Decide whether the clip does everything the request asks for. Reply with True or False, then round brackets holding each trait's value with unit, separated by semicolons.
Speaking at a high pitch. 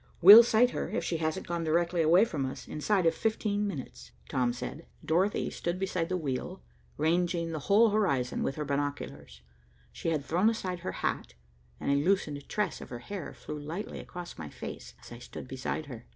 False (165 Hz)